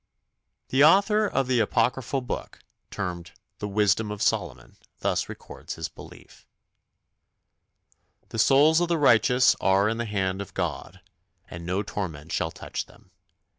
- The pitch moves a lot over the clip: Yes, wide, 5.9 semitones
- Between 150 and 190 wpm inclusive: No, average, 140 wpm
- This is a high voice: No, low, 110 Hz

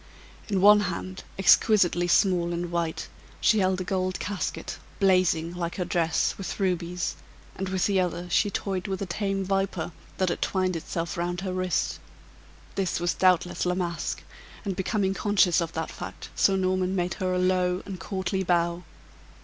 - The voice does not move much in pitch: Yes, narrow, 1.6 semitones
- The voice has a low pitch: No, medium, 185 Hz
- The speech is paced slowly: No, average, 170 wpm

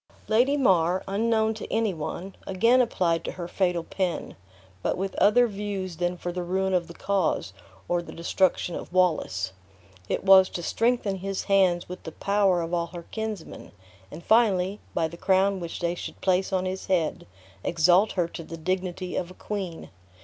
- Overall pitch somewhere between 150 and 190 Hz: Yes, medium, 185 Hz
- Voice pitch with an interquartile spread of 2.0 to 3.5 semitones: Yes, narrow, 2.4 semitones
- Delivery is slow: No, average, 180 wpm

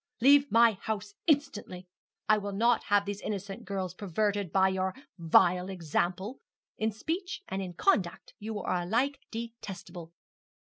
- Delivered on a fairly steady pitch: No, average, 3.6 semitones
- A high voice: Yes, high, 200 Hz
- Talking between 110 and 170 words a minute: Yes, average, 140 wpm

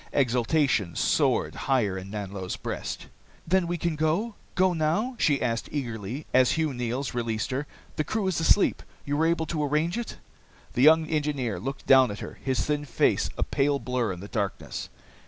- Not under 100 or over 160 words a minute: No, average, 180 wpm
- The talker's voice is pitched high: No, medium, 140 Hz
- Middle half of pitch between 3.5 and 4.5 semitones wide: No, average, 5.3 semitones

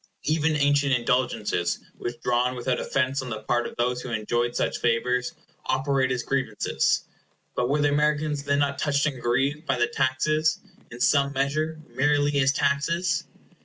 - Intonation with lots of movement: No, average, 2.8 semitones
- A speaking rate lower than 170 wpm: Yes, average, 160 wpm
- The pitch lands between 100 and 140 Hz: Yes, low, 135 Hz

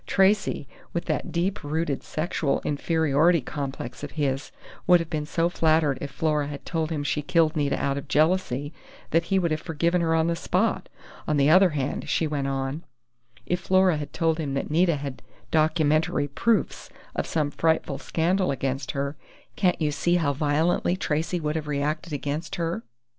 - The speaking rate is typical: Yes, average, 180 wpm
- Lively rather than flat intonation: No, average, 2.8 semitones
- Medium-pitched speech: Yes, medium, 155 Hz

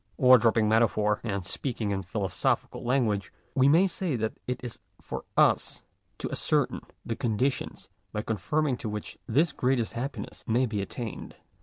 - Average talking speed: Yes, average, 165 wpm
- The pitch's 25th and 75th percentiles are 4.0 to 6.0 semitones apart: No, average, 3.5 semitones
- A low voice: Yes, low, 115 Hz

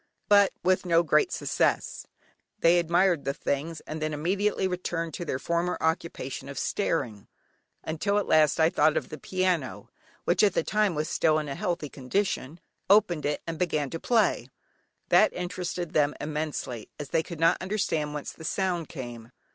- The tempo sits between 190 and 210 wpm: No, average, 170 wpm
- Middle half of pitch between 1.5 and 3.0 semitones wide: No, average, 3.4 semitones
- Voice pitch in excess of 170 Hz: No, medium, 165 Hz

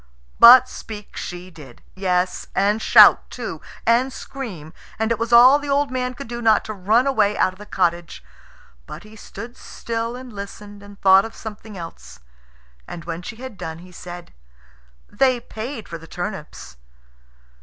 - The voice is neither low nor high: No, high, 210 Hz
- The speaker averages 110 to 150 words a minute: No, average, 170 wpm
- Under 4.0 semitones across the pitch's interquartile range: No, average, 4.7 semitones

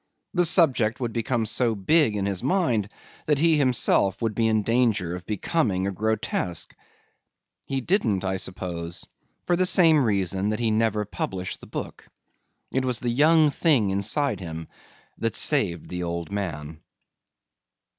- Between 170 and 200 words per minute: No, average, 155 wpm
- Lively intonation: Yes, wide, 5.7 semitones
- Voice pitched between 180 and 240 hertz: No, low, 110 Hz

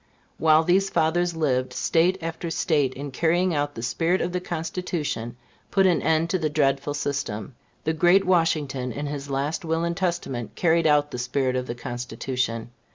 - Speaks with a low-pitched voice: No, medium, 155 Hz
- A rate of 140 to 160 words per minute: No, average, 175 wpm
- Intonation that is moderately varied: Yes, average, 4.5 semitones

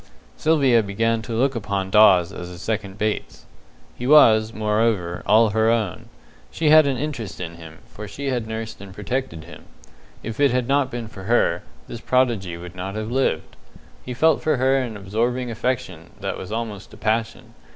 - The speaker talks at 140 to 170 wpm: No, average, 185 wpm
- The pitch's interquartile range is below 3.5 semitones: No, average, 4.1 semitones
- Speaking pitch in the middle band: No, low, 110 Hz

